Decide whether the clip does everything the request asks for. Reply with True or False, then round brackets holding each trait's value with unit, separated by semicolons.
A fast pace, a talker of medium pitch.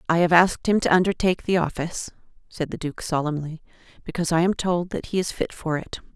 True (215 wpm; 170 Hz)